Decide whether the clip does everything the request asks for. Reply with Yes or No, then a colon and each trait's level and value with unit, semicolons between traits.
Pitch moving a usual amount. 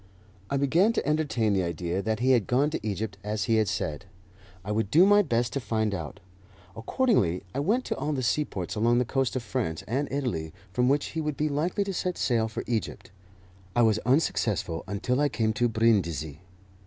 No: wide, 5.7 semitones